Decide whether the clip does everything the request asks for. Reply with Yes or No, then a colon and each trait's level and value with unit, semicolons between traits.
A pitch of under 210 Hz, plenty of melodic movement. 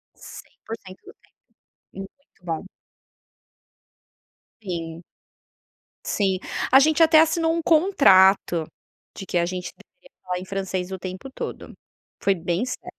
Yes: high, 190 Hz; wide, 7.8 semitones